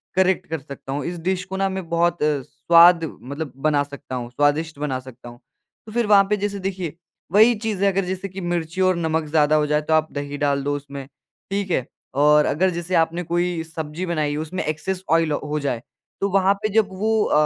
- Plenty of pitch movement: No, average, 4.4 semitones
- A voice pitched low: No, medium, 165 Hz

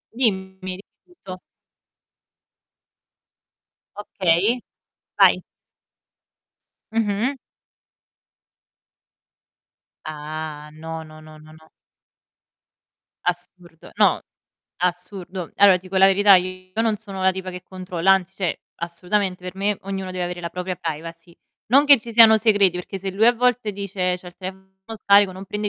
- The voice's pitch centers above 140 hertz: Yes, medium, 185 Hz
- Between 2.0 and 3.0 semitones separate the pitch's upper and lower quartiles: Yes, narrow, 2.4 semitones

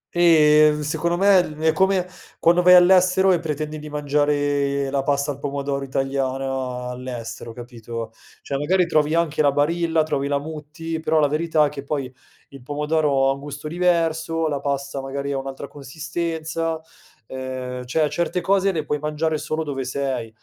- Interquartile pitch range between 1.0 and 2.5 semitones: No, average, 2.9 semitones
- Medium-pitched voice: Yes, medium, 150 Hz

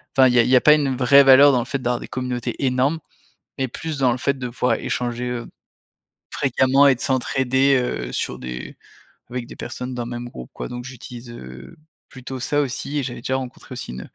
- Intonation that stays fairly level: Yes, narrow, 1.7 semitones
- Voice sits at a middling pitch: No, low, 125 Hz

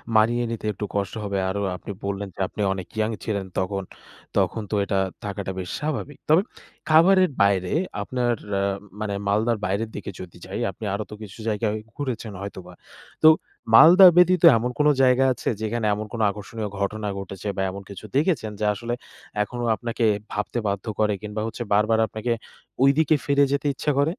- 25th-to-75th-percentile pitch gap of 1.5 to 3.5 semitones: No, average, 3.9 semitones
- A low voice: Yes, low, 110 Hz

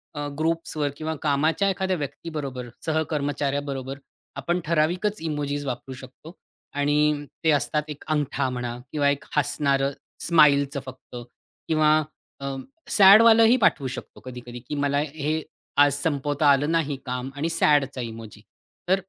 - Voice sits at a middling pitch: Yes, medium, 145 Hz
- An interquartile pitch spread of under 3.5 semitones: Yes, narrow, 2.5 semitones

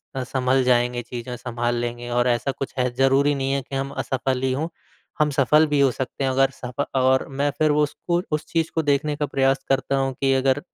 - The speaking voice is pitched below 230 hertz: Yes, low, 135 Hz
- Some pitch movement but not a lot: No, narrow, 2.0 semitones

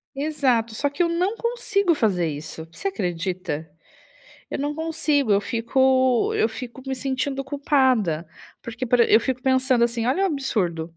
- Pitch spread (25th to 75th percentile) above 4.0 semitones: Yes, average, 4.7 semitones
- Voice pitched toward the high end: Yes, very high, 260 Hz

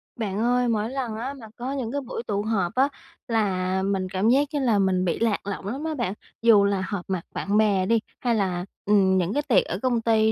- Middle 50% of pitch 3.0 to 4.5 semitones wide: Yes, average, 4.0 semitones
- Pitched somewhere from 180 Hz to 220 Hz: Yes, high, 215 Hz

